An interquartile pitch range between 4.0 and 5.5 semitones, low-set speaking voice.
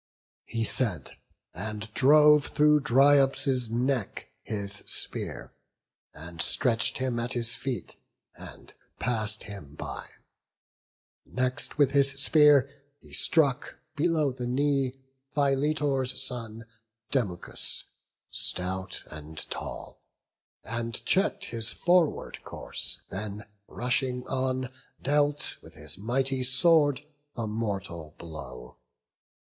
Yes: average, 4.6 semitones; low, 125 Hz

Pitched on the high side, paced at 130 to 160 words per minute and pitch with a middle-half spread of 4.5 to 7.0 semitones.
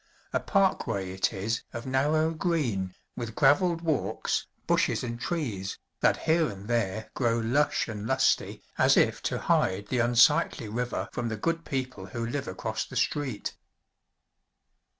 No: low, 120 Hz; average, 150 wpm; wide, 5.6 semitones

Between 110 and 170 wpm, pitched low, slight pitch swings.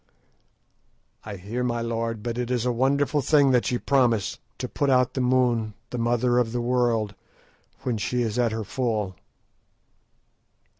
Yes: average, 160 wpm; low, 120 Hz; narrow, 1.9 semitones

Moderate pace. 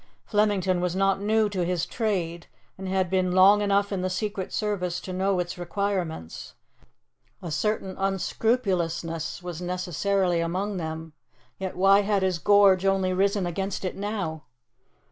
Yes: average, 145 wpm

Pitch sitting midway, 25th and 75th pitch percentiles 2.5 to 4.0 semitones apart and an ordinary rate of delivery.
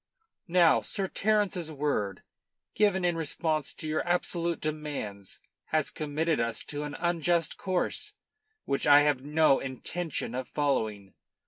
No: medium, 155 Hz; average, 3.7 semitones; slow, 130 wpm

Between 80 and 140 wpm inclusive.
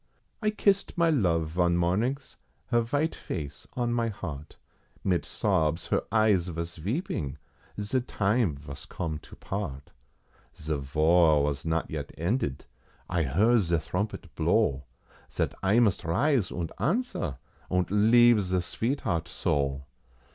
Yes: slow, 135 wpm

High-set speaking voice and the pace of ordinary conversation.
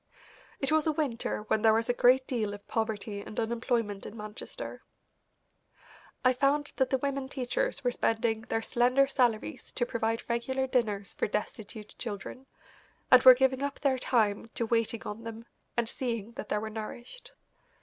Yes: high, 235 Hz; average, 170 wpm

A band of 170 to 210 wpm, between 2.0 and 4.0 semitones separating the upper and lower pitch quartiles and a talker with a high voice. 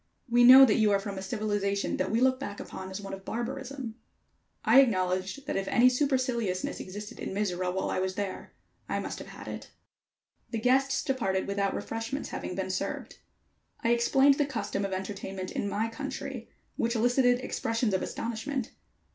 No: average, 180 wpm; average, 4.5 semitones; high, 225 Hz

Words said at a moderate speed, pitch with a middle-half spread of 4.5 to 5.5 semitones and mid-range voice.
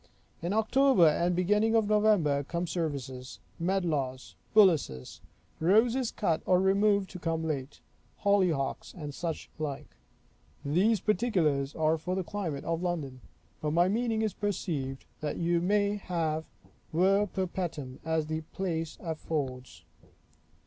No: slow, 130 wpm; average, 4.8 semitones; medium, 170 Hz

